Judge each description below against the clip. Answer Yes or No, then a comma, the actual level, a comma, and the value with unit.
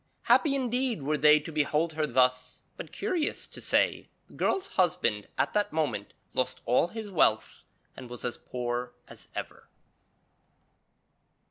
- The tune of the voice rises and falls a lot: Yes, wide, 8.6 semitones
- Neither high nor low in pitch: Yes, medium, 150 Hz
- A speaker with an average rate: Yes, average, 145 wpm